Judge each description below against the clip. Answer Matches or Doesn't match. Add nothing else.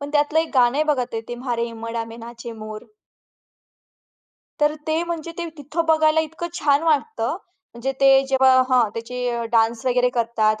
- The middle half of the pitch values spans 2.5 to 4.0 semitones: Doesn't match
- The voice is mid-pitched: Doesn't match